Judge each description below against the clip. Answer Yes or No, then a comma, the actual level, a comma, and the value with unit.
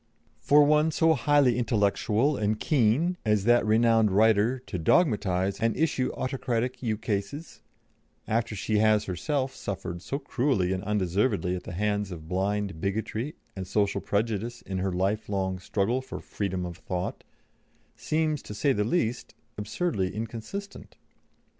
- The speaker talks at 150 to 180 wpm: No, average, 140 wpm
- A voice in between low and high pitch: No, low, 110 Hz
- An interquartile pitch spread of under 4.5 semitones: No, average, 4.8 semitones